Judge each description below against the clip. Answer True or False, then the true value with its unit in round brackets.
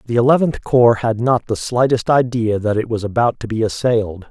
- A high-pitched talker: False (115 Hz)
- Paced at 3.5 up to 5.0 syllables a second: False (5.4 syllables/s)